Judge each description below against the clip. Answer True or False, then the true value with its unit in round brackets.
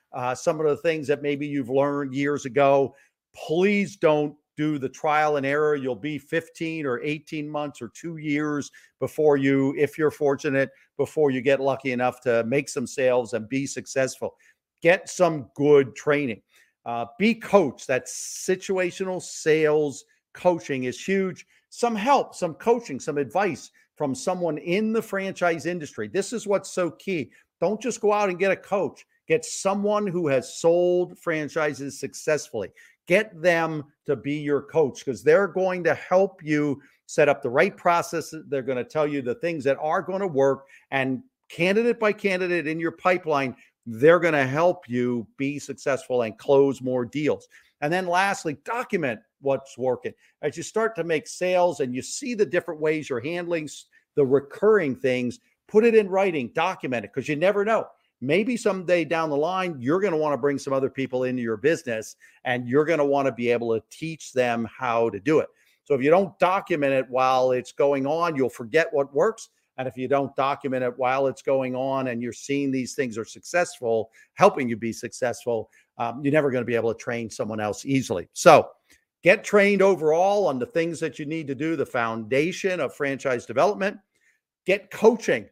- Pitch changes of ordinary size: True (4.9 semitones)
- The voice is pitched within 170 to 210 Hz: False (150 Hz)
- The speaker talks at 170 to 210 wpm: True (185 wpm)